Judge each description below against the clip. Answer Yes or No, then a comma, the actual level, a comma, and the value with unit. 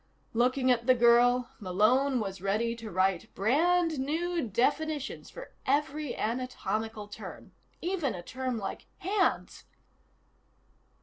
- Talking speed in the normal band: No, slow, 115 wpm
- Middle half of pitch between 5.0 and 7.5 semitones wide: Yes, wide, 5.4 semitones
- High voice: Yes, very high, 250 Hz